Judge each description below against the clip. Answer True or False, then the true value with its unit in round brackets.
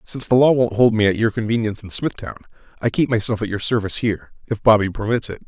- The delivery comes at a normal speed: False (230 wpm)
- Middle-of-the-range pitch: False (110 Hz)